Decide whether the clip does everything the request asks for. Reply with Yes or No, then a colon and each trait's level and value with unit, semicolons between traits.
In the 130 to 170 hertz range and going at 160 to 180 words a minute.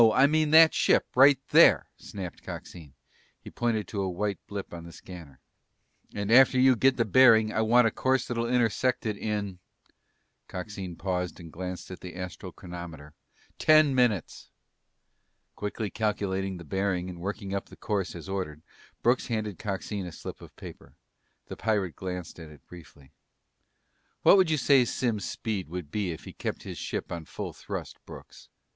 No: low, 100 Hz; average, 170 wpm